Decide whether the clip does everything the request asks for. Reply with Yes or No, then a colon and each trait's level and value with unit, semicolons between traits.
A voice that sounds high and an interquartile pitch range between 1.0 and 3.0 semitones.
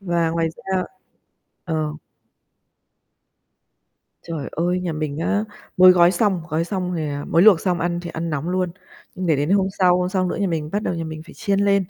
No: medium, 175 Hz; narrow, 2.4 semitones